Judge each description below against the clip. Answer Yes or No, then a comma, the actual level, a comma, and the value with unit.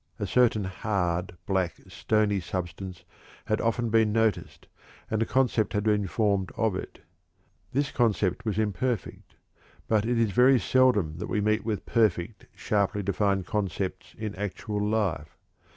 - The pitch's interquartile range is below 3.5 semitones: Yes, average, 2.9 semitones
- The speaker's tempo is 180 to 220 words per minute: No, average, 145 wpm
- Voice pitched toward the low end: Yes, low, 105 Hz